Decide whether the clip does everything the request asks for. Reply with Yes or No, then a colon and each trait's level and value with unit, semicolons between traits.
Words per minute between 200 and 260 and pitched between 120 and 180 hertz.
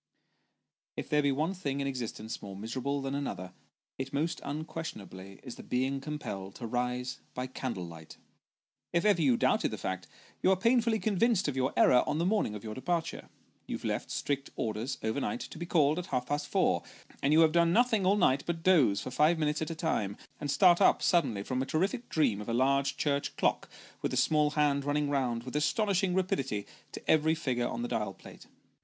Yes: fast, 205 wpm; medium, 140 Hz